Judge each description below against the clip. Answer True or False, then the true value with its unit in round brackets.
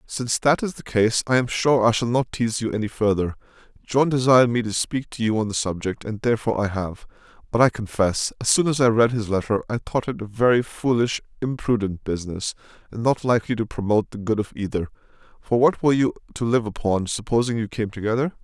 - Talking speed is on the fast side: True (220 wpm)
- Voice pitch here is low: True (115 Hz)